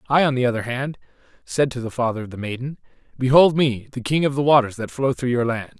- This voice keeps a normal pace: No, fast, 250 wpm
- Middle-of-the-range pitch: No, low, 130 Hz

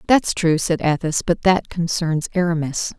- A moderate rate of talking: Yes, average, 160 wpm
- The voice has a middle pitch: Yes, medium, 170 Hz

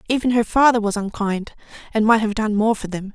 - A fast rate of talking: Yes, fast, 230 wpm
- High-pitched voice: Yes, high, 215 Hz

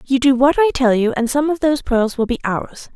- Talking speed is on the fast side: Yes, fast, 285 wpm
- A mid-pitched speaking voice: No, very high, 260 Hz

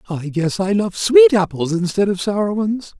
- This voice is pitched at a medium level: Yes, medium, 180 Hz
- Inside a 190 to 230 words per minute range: Yes, average, 200 wpm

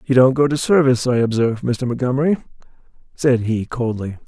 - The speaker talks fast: No, average, 170 wpm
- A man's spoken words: Yes, male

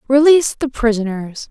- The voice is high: Yes, very high, 250 Hz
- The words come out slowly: Yes, slow, 120 wpm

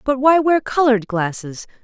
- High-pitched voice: Yes, very high, 250 Hz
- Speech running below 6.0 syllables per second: Yes, 5.0 syllables/s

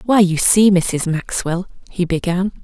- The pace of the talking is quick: No, average, 160 wpm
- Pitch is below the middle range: No, medium, 185 Hz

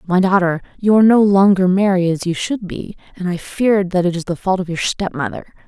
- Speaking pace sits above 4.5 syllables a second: Yes, 5.5 syllables/s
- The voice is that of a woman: Yes, female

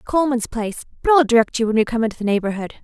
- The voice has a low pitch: No, high, 235 Hz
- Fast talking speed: Yes, fast, 255 wpm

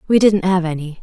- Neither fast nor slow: No, fast, 235 wpm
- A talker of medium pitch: Yes, medium, 180 Hz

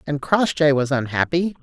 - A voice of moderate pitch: Yes, medium, 150 Hz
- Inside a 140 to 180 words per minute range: Yes, average, 150 wpm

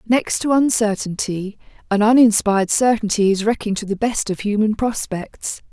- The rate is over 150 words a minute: No, average, 145 wpm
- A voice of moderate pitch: No, high, 215 Hz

